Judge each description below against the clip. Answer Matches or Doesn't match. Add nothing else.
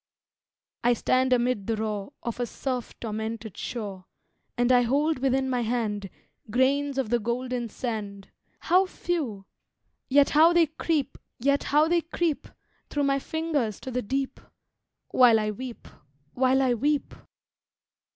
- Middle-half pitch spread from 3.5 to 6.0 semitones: Matches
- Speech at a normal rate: Doesn't match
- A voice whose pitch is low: Doesn't match